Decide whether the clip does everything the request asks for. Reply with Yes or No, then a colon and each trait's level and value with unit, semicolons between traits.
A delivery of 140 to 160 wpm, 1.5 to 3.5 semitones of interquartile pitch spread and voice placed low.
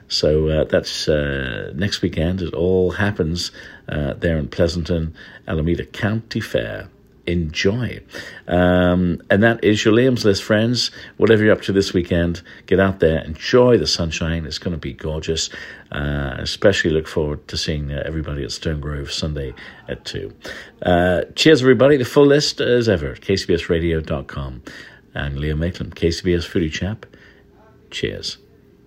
No: average, 150 wpm; average, 4.2 semitones; very low, 85 Hz